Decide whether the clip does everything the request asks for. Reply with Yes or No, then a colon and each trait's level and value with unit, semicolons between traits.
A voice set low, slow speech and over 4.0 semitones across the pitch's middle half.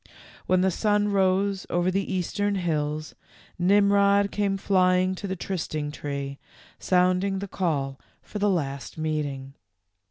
No: medium, 185 Hz; slow, 130 wpm; average, 4.4 semitones